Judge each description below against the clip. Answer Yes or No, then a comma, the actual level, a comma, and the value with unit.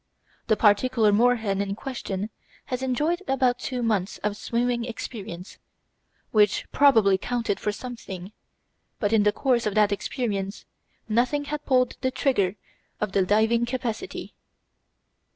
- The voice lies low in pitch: No, high, 225 Hz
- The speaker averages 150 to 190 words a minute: No, slow, 135 wpm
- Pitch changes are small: No, average, 3.6 semitones